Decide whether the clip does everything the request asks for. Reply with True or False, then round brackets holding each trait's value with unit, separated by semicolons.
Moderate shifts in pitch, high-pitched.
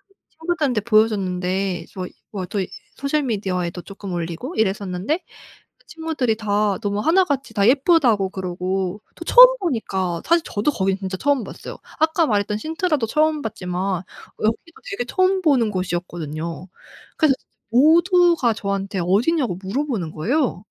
False (8.1 semitones; 215 Hz)